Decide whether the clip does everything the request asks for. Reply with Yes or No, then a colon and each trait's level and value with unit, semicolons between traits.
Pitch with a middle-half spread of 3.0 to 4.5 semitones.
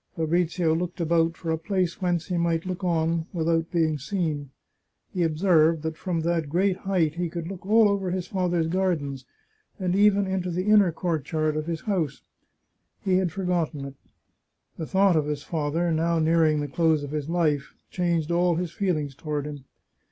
No: narrow, 2.5 semitones